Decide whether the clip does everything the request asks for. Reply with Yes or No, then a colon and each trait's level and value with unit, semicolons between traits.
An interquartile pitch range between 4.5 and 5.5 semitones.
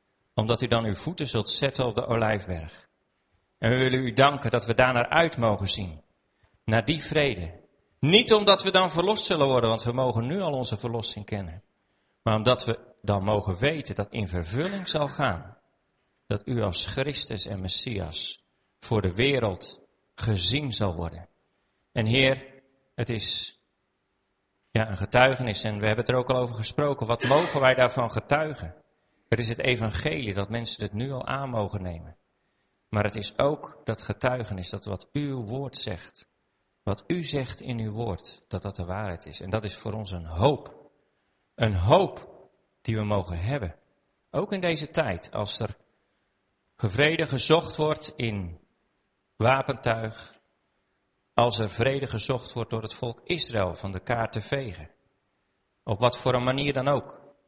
Yes: average, 4.9 semitones